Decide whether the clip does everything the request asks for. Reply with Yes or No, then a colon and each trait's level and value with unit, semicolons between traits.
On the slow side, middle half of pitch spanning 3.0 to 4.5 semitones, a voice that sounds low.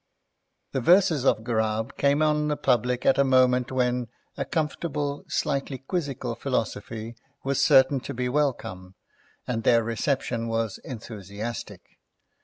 Yes: slow, 130 wpm; average, 3.5 semitones; low, 125 Hz